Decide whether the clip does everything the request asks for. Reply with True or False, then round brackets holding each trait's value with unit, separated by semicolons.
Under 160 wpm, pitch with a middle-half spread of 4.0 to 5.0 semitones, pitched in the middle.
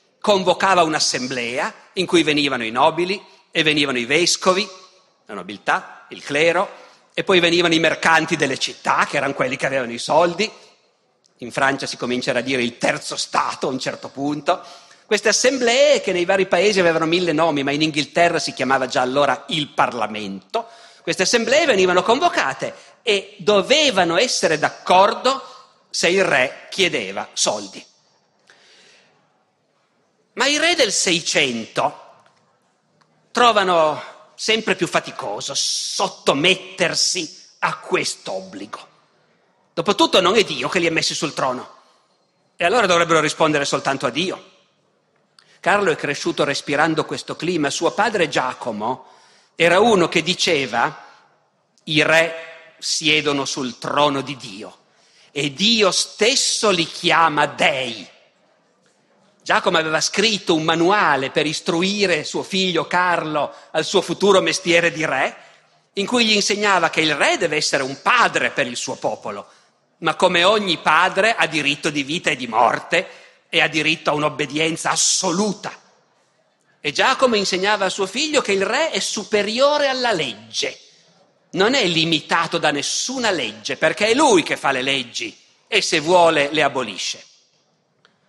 True (140 wpm; 4.6 semitones; 170 Hz)